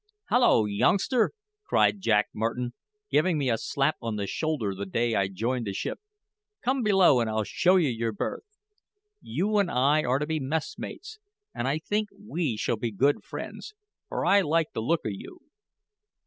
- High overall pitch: No, medium, 140 Hz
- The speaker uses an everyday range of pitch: No, wide, 8.4 semitones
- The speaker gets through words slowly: No, average, 175 wpm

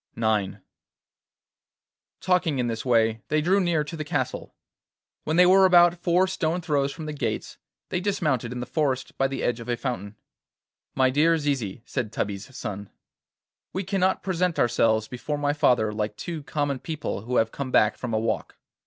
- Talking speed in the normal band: Yes, average, 180 wpm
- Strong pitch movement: Yes, wide, 6.3 semitones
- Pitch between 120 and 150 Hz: Yes, medium, 140 Hz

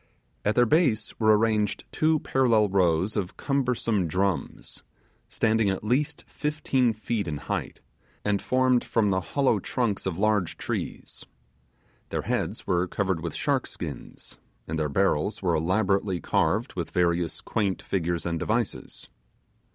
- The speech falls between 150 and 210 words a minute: No, average, 140 wpm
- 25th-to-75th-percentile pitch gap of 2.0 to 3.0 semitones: No, average, 4.5 semitones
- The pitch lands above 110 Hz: No, low, 105 Hz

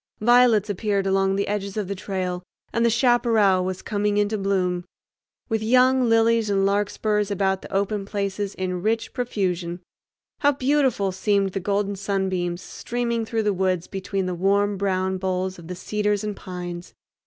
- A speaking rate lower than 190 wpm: Yes, average, 165 wpm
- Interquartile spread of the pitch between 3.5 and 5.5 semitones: No, narrow, 2.5 semitones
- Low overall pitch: No, high, 200 Hz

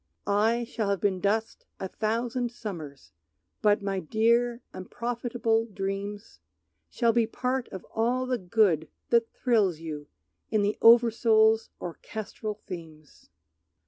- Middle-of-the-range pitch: No, high, 220 Hz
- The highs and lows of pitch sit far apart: No, average, 3.3 semitones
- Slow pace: Yes, slow, 120 wpm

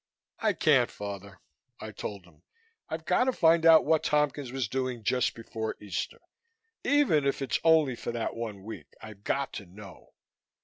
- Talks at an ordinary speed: Yes, average, 170 wpm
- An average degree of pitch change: No, wide, 6.8 semitones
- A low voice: Yes, low, 125 Hz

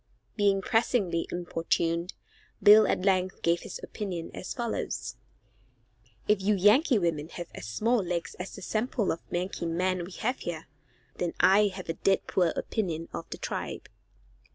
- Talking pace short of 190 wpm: Yes, average, 160 wpm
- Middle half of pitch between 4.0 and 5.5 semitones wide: No, average, 3.6 semitones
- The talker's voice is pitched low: No, medium, 185 Hz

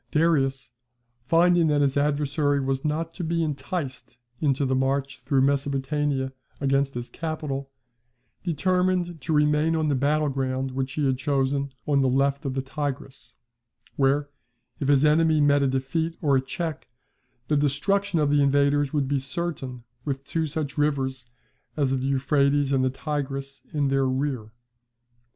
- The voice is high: No, medium, 140 Hz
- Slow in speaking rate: No, average, 155 wpm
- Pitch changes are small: Yes, narrow, 2.1 semitones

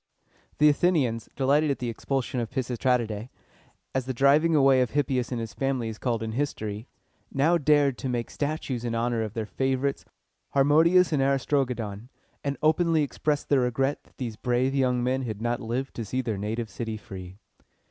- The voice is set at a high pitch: No, low, 130 Hz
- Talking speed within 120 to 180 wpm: No, average, 190 wpm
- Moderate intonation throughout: Yes, average, 3.4 semitones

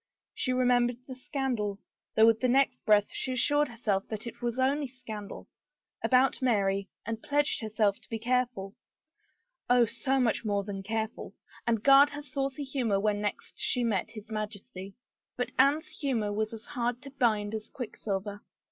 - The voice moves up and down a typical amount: Yes, average, 3.7 semitones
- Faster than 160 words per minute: Yes, average, 180 wpm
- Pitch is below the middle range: No, high, 235 Hz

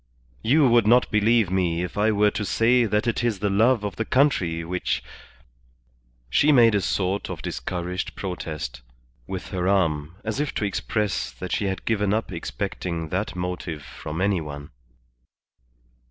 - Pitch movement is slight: No, average, 4.5 semitones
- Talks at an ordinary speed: Yes, average, 170 wpm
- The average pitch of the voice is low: Yes, very low, 95 Hz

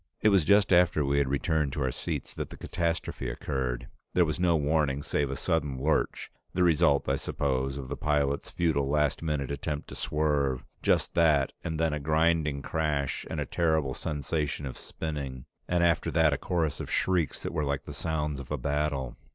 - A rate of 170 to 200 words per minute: Yes, average, 190 wpm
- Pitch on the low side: Yes, very low, 75 Hz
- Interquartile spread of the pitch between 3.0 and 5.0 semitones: No, narrow, 2.6 semitones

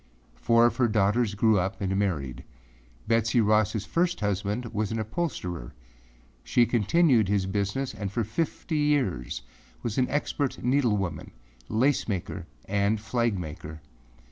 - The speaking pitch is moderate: No, low, 110 Hz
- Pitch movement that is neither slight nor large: Yes, average, 3.7 semitones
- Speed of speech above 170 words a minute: No, slow, 135 wpm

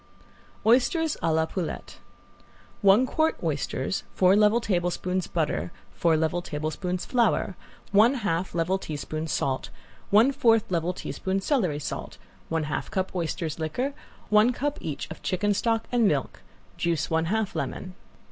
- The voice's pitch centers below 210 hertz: Yes, medium, 185 Hz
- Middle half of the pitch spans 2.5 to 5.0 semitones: No, wide, 5.5 semitones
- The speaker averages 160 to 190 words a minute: No, average, 140 wpm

